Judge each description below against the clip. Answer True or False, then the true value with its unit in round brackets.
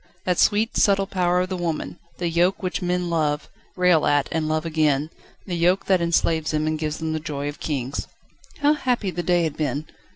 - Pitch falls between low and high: True (170 Hz)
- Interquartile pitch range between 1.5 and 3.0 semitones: True (2.7 semitones)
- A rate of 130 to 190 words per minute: False (205 wpm)